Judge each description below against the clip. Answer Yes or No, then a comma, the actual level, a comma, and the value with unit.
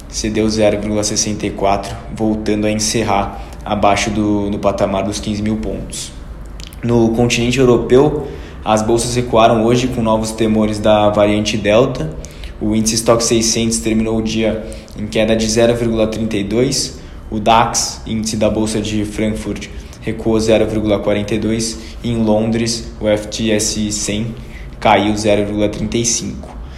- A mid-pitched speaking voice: No, low, 110 Hz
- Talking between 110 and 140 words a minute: Yes, slow, 120 wpm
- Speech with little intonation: Yes, narrow, 1.5 semitones